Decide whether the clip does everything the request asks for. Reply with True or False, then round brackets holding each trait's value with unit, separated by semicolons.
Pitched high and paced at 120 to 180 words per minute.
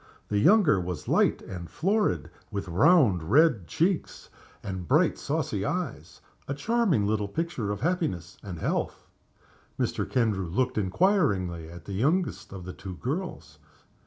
False (105 Hz; 140 wpm)